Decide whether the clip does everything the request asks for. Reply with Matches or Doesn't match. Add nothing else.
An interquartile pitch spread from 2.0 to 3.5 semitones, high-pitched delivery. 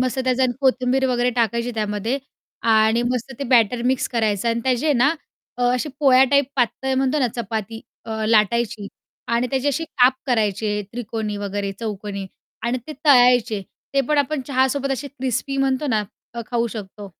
Matches